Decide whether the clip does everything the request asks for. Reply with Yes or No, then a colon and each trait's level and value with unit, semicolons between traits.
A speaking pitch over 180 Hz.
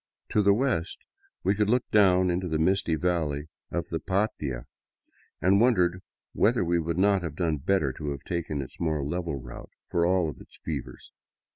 No: very low, 85 Hz